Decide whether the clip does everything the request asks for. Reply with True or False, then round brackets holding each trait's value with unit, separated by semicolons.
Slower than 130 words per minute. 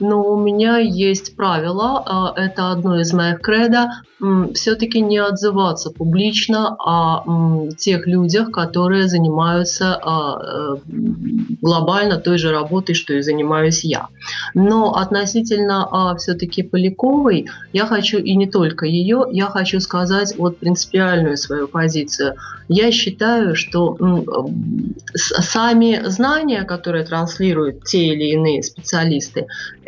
True (110 wpm)